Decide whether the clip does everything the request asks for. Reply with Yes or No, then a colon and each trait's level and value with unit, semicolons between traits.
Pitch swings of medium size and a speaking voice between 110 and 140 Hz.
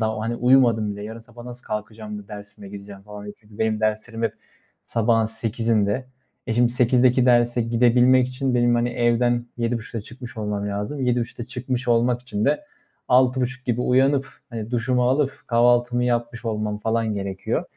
No: narrow, 2.3 semitones; low, 120 Hz